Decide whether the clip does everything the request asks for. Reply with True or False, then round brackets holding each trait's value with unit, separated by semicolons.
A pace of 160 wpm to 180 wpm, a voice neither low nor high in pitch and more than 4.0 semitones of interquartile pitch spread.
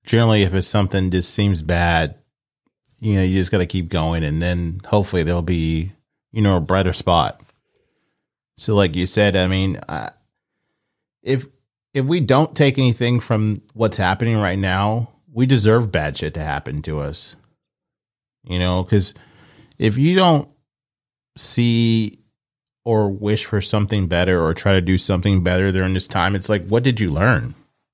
False (170 wpm; 105 Hz; 4.7 semitones)